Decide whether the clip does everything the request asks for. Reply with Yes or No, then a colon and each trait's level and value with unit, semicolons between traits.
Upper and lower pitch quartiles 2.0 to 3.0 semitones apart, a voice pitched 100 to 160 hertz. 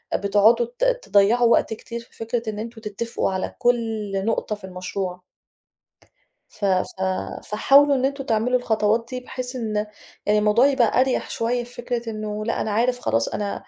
No: average, 2.7 semitones; high, 230 Hz